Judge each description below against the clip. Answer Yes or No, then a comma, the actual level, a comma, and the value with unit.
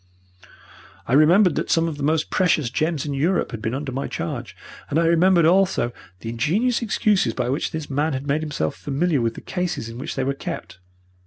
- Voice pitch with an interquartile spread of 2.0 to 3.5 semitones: No, average, 4.4 semitones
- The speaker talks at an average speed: No, fast, 210 wpm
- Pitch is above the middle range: No, medium, 150 Hz